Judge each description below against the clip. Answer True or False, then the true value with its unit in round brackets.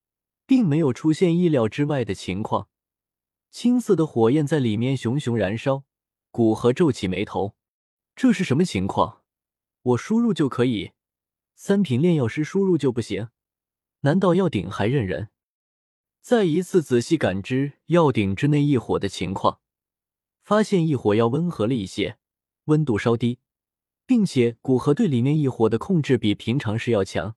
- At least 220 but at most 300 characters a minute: True (235 characters per minute)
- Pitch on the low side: True (130 Hz)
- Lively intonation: True (6.5 semitones)